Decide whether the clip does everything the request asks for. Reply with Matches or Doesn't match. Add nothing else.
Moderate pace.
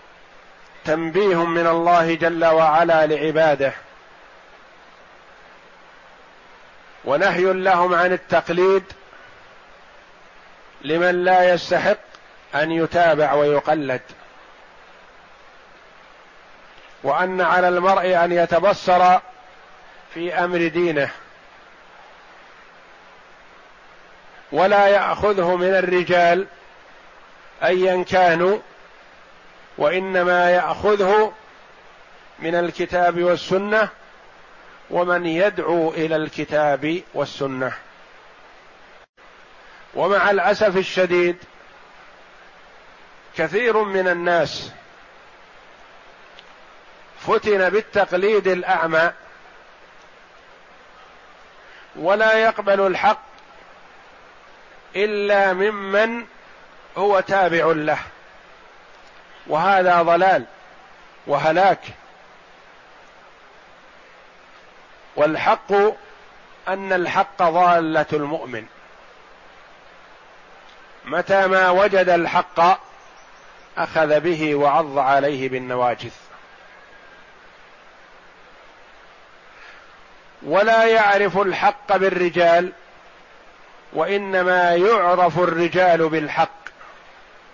Doesn't match